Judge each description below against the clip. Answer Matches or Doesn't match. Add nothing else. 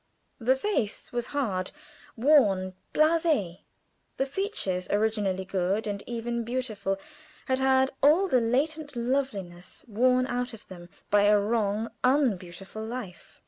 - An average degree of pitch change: Matches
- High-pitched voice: Matches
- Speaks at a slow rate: Matches